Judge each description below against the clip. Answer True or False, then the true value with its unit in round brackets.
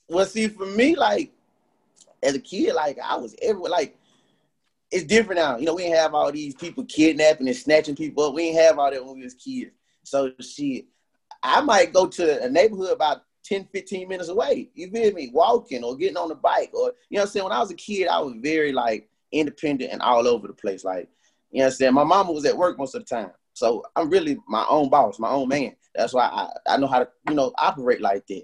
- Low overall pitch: False (180 Hz)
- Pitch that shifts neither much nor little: False (8.8 semitones)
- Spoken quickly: True (245 wpm)